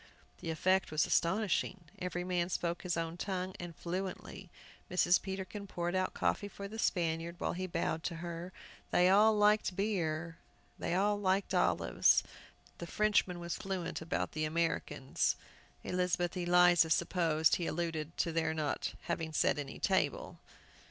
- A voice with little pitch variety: Yes, narrow, 2.2 semitones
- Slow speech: No, average, 150 wpm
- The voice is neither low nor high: Yes, medium, 175 Hz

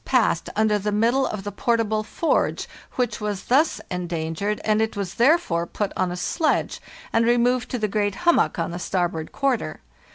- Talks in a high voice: Yes, high, 210 Hz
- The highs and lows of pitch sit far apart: No, average, 4.7 semitones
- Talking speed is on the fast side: No, average, 185 wpm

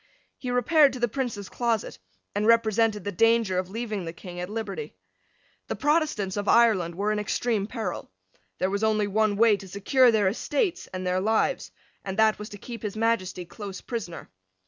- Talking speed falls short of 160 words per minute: No, average, 185 wpm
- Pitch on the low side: No, high, 215 Hz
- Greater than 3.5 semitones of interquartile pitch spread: No, average, 3.0 semitones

